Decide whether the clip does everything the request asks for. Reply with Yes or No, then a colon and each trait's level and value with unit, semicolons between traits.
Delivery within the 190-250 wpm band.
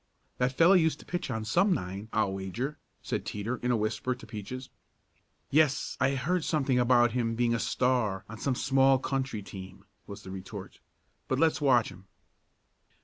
No: average, 175 wpm